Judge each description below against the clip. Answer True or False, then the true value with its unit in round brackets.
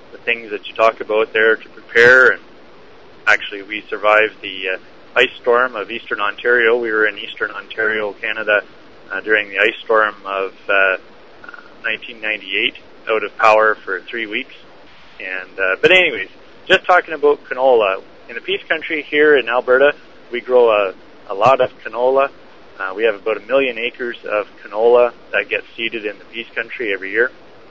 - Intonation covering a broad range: True (5.9 semitones)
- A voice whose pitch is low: True (115 Hz)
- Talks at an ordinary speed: True (170 wpm)